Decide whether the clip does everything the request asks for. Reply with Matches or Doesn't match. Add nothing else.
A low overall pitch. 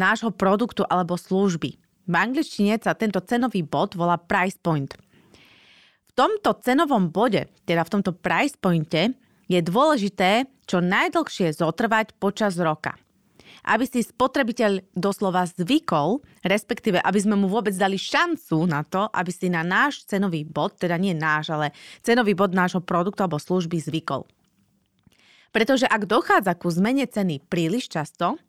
Doesn't match